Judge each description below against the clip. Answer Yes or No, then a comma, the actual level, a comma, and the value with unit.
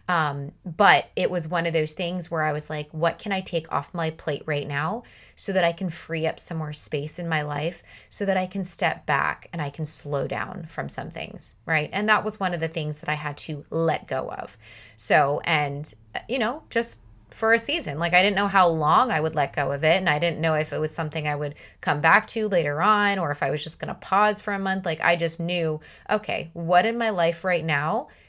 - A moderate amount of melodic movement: Yes, average, 3.6 semitones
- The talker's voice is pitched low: No, medium, 165 Hz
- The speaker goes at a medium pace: No, fast, 250 wpm